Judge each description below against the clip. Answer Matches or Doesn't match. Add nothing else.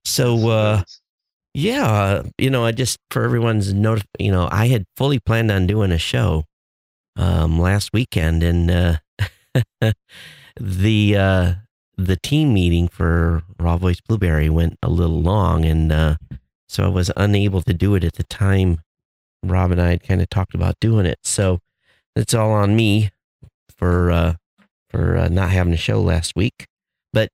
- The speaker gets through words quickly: Doesn't match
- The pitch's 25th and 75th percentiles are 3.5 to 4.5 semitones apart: Matches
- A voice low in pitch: Matches